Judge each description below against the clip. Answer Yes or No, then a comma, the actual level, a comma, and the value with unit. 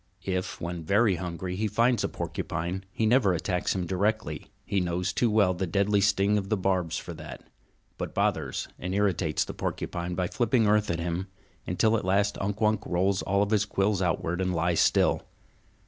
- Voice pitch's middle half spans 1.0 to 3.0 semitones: Yes, average, 2.7 semitones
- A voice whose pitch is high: No, very low, 95 Hz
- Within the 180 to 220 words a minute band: Yes, average, 185 wpm